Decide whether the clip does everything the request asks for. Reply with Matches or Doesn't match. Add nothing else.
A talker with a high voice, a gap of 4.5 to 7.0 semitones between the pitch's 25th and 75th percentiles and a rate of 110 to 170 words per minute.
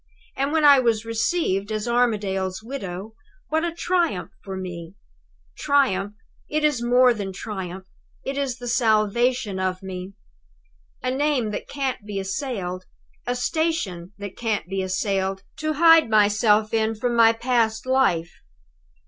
Matches